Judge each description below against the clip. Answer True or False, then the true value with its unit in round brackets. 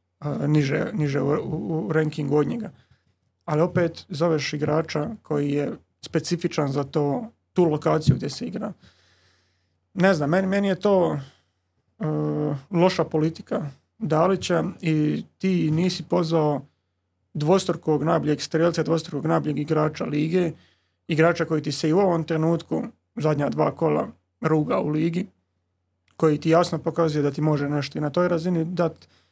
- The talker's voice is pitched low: False (155 Hz)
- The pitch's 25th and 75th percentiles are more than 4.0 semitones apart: False (2.9 semitones)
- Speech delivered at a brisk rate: False (145 wpm)